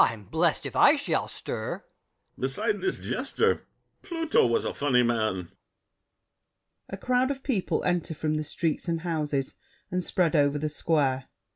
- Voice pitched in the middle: Yes, medium, 160 Hz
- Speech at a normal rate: Yes, average, 155 wpm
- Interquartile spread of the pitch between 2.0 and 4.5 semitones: No, average, 5.1 semitones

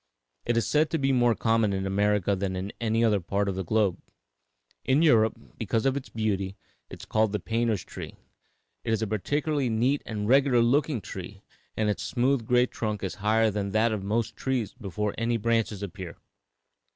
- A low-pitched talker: Yes, low, 110 Hz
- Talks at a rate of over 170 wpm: Yes, average, 190 wpm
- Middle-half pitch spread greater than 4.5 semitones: No, average, 2.9 semitones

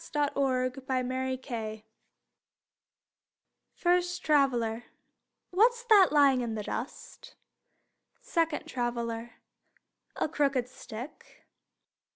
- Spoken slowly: Yes, slow, 80 wpm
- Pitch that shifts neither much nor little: Yes, average, 4.0 semitones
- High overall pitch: Yes, very high, 260 Hz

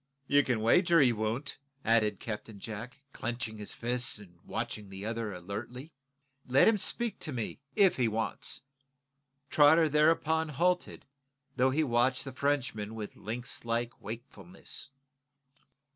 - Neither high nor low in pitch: No, low, 120 Hz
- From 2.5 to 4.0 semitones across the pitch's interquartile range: No, average, 4.8 semitones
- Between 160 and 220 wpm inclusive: No, slow, 135 wpm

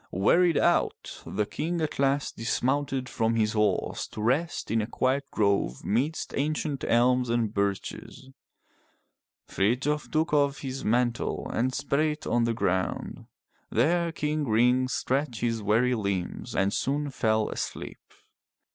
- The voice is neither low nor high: No, low, 125 Hz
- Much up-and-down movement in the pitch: No, average, 4.6 semitones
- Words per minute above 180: No, average, 140 wpm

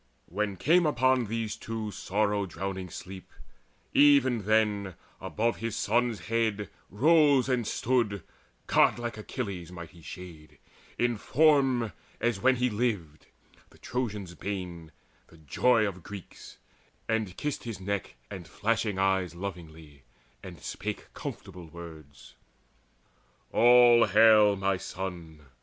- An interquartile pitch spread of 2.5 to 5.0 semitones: Yes, average, 4.6 semitones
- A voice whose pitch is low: Yes, low, 105 Hz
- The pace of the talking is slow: Yes, slow, 115 wpm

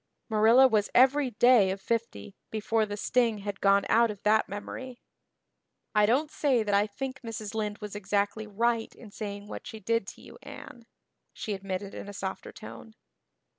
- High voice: Yes, high, 215 Hz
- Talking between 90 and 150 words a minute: No, average, 175 wpm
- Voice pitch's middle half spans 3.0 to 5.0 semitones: No, narrow, 2.4 semitones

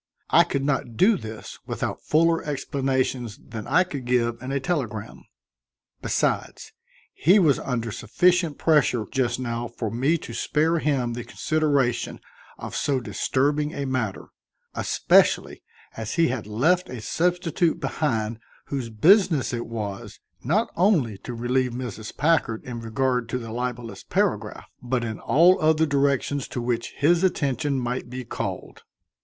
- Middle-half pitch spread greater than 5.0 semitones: No, average, 4.7 semitones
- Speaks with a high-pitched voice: No, low, 130 Hz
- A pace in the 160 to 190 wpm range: No, average, 145 wpm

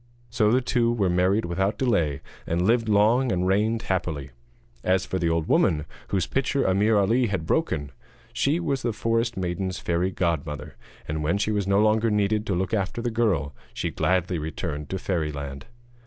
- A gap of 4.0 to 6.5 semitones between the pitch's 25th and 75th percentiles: Yes, average, 4.8 semitones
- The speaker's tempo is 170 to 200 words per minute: Yes, average, 180 wpm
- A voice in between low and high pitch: No, very low, 95 Hz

